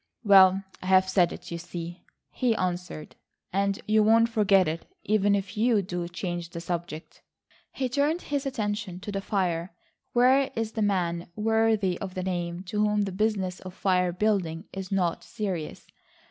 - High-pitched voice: Yes, high, 195 Hz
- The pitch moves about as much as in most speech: Yes, average, 3.3 semitones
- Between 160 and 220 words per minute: Yes, average, 165 wpm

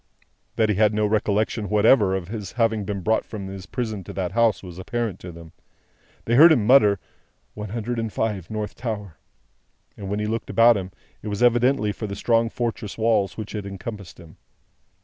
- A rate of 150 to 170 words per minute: No, average, 200 wpm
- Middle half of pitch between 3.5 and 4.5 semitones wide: No, narrow, 2.6 semitones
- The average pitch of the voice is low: Yes, low, 105 Hz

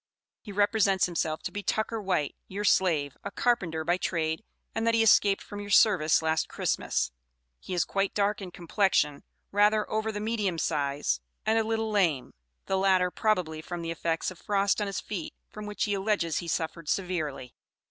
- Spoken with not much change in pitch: No, average, 4.1 semitones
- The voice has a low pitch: No, high, 190 Hz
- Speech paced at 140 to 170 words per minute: No, average, 185 wpm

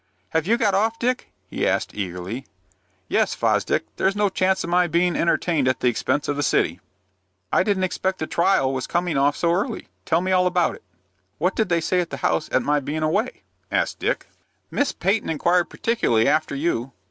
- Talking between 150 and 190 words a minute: No, average, 200 wpm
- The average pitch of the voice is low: No, medium, 170 Hz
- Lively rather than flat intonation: No, average, 4.7 semitones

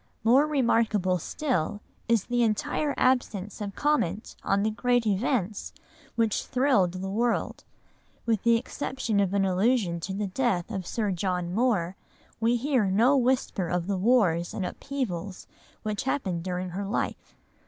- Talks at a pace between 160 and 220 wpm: No, average, 150 wpm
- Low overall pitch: No, high, 210 Hz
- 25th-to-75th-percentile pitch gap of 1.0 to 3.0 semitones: No, average, 4.7 semitones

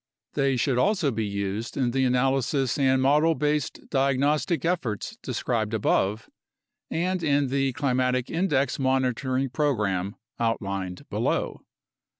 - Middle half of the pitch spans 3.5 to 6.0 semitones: Yes, average, 3.9 semitones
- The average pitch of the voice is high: No, low, 130 Hz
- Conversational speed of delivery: No, slow, 125 wpm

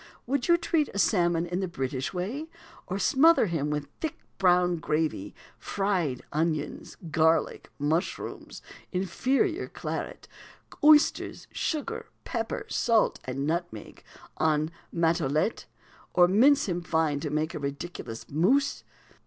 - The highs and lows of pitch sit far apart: Yes, wide, 6.7 semitones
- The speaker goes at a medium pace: No, slow, 120 wpm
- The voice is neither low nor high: Yes, medium, 175 Hz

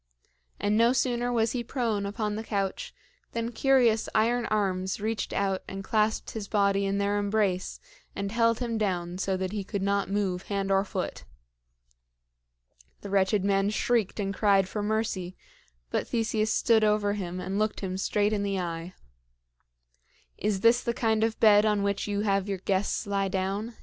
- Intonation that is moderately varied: No, narrow, 2.1 semitones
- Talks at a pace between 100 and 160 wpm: No, average, 175 wpm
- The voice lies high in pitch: Yes, high, 205 Hz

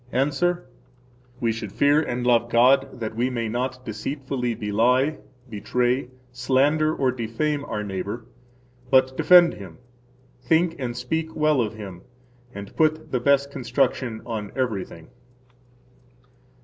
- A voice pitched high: No, low, 125 Hz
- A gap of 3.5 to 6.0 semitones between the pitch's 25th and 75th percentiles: Yes, average, 3.9 semitones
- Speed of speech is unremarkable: No, slow, 125 wpm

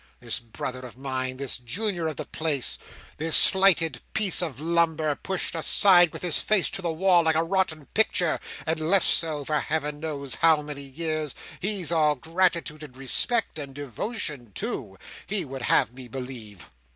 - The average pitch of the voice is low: No, medium, 155 Hz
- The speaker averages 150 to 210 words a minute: Yes, average, 170 wpm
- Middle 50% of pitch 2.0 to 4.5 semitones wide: Yes, average, 4.2 semitones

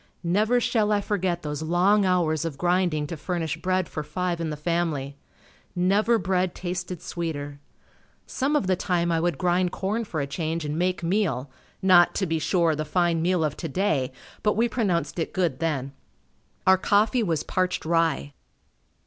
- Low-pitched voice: No, medium, 175 Hz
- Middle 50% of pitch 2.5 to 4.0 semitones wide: Yes, average, 2.9 semitones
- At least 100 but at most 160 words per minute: No, average, 175 wpm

